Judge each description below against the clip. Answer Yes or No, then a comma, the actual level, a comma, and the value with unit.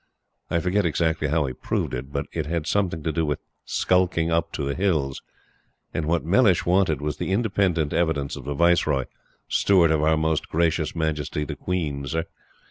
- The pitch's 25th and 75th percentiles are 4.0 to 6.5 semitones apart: No, narrow, 2.6 semitones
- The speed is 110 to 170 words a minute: No, average, 185 wpm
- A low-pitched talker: Yes, very low, 80 Hz